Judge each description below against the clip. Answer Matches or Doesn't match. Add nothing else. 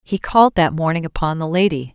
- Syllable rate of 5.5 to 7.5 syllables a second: Matches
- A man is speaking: Doesn't match